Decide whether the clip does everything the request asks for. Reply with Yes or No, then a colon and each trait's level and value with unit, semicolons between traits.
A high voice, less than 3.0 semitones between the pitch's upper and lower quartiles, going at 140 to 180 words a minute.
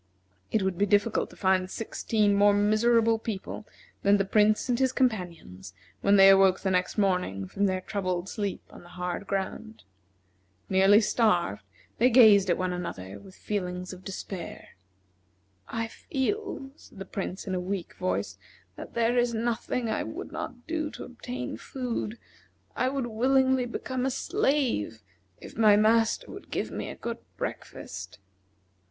No: high, 205 Hz; average, 4.2 semitones; average, 160 wpm